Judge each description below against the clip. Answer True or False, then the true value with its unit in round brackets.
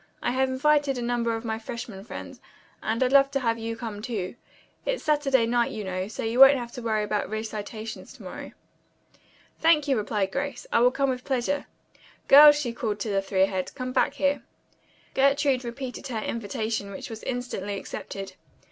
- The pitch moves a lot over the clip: False (3.9 semitones)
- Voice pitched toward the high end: True (235 Hz)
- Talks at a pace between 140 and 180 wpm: False (190 wpm)